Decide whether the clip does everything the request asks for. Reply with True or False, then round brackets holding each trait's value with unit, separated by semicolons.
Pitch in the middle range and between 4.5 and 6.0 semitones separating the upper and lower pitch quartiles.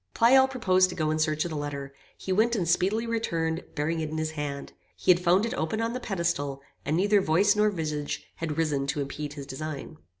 True (165 Hz; 5.0 semitones)